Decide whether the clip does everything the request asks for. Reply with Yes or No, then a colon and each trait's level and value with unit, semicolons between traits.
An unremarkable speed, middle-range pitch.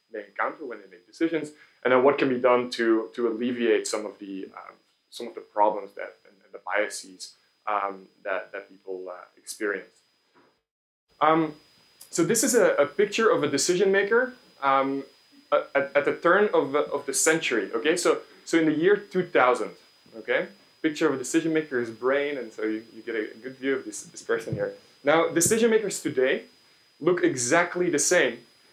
Yes: average, 190 wpm; medium, 160 Hz